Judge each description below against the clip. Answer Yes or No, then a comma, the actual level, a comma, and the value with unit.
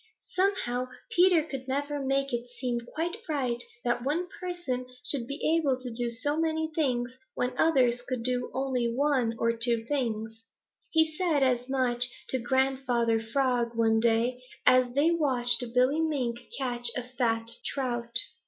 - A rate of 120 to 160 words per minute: Yes, average, 155 wpm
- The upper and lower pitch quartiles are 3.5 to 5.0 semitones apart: No, average, 3.0 semitones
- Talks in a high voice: Yes, very high, 255 Hz